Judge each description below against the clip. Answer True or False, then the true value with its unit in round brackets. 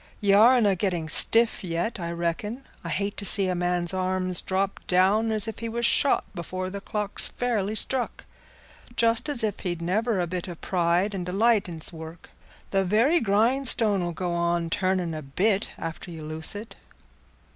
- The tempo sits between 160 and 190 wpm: True (180 wpm)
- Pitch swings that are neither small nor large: True (4.0 semitones)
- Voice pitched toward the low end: False (190 Hz)